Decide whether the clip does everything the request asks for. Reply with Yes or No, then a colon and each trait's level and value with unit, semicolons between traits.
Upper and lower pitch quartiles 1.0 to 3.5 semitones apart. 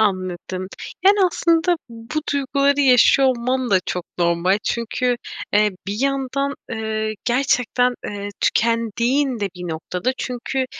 No: average, 4.8 semitones